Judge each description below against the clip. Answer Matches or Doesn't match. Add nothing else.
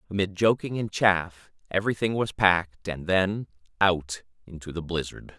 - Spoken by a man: Matches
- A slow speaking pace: Doesn't match